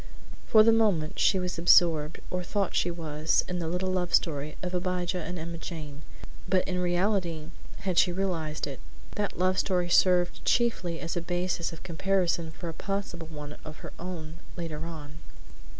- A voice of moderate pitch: Yes, medium, 175 Hz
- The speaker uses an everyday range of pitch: No, narrow, 2.3 semitones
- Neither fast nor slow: Yes, average, 175 wpm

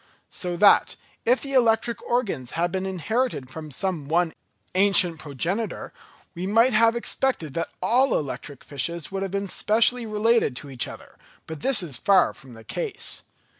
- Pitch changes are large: Yes, wide, 6.3 semitones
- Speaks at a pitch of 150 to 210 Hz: Yes, high, 190 Hz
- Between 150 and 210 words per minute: Yes, average, 165 wpm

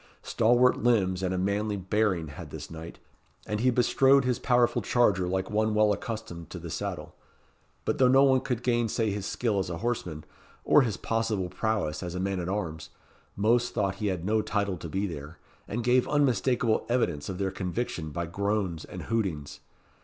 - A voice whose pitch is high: No, low, 105 Hz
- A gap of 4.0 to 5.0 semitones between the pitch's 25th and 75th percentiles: Yes, average, 4.6 semitones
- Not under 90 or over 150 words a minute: No, average, 185 wpm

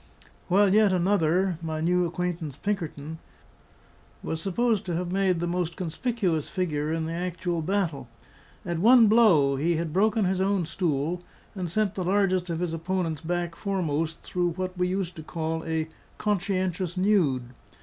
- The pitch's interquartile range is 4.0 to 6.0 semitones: No, average, 2.9 semitones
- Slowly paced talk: No, average, 160 wpm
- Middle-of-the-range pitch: Yes, medium, 175 Hz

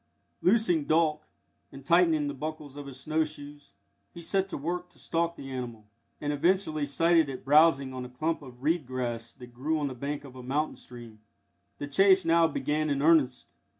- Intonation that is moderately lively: Yes, average, 3.8 semitones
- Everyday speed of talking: Yes, average, 190 wpm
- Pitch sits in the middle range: Yes, medium, 145 Hz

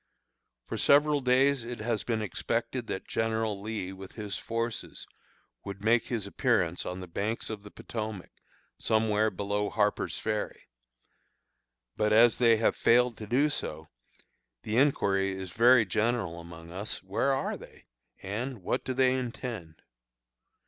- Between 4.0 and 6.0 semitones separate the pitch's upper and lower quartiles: No, average, 3.3 semitones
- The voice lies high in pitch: No, low, 110 Hz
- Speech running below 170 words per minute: Yes, average, 145 wpm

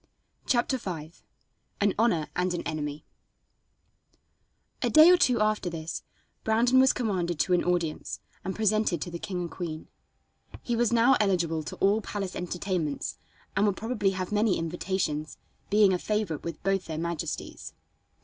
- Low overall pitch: No, medium, 185 Hz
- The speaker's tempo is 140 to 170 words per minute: Yes, average, 155 wpm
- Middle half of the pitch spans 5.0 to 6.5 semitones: No, average, 4.2 semitones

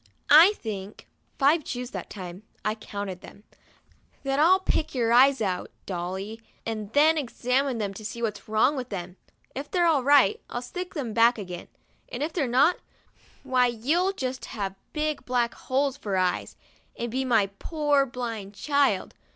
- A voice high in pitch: Yes, high, 245 Hz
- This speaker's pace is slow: No, average, 165 wpm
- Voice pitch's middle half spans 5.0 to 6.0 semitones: Yes, average, 5.3 semitones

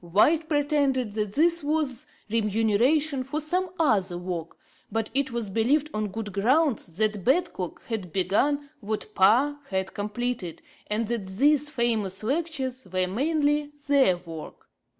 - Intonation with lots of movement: Yes, wide, 6.2 semitones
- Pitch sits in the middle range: No, high, 235 Hz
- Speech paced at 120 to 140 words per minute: Yes, slow, 135 wpm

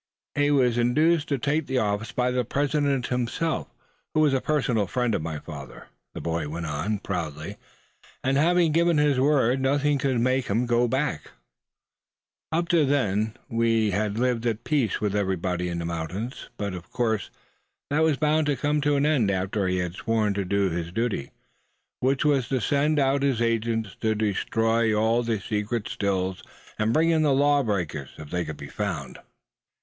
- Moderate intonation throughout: No, wide, 6.0 semitones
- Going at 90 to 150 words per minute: No, average, 185 wpm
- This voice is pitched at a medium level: No, low, 115 Hz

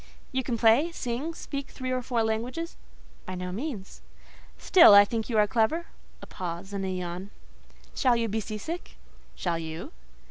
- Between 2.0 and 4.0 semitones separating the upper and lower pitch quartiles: No, average, 5.1 semitones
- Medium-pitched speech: No, high, 225 Hz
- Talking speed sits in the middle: Yes, average, 175 wpm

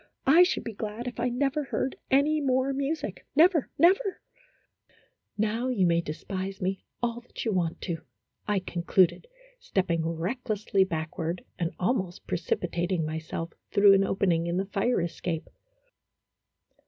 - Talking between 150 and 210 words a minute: No, average, 140 wpm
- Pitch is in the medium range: No, high, 195 Hz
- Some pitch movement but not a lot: No, wide, 6.7 semitones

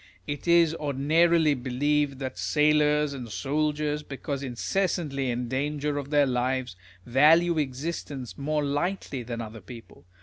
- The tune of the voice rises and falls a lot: No, average, 2.7 semitones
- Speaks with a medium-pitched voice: Yes, medium, 145 Hz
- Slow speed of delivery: Yes, slow, 130 wpm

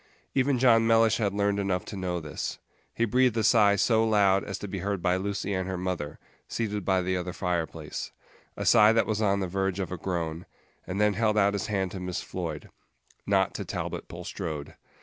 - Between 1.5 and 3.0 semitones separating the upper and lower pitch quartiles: Yes, average, 2.7 semitones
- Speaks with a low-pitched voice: Yes, low, 100 Hz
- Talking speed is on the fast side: Yes, fast, 210 wpm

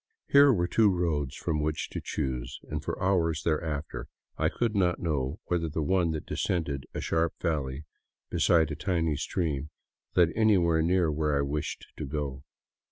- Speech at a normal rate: Yes, average, 170 wpm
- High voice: No, very low, 80 Hz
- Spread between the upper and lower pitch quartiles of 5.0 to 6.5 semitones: No, average, 3.2 semitones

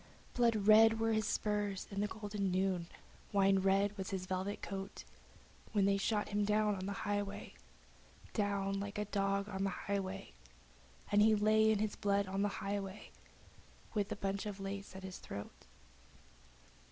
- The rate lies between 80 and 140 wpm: No, average, 165 wpm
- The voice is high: Yes, high, 200 Hz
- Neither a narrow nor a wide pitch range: No, narrow, 1.2 semitones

